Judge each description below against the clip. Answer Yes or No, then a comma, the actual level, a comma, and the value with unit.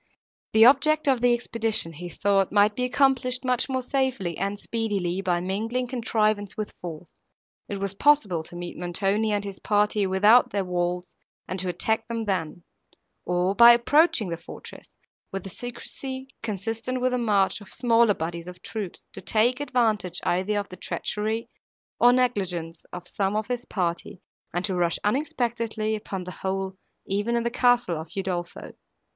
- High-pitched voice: Yes, high, 210 Hz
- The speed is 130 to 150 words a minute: No, average, 165 wpm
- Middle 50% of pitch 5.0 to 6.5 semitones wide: No, average, 4.6 semitones